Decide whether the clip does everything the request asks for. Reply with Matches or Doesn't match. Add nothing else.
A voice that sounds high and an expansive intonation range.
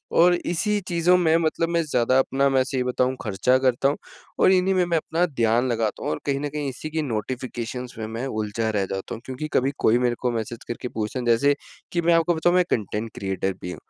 Doesn't match